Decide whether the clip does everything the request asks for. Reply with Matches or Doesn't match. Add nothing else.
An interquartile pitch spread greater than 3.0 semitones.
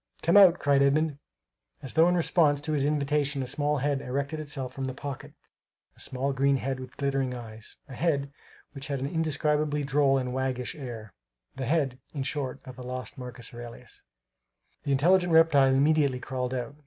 Doesn't match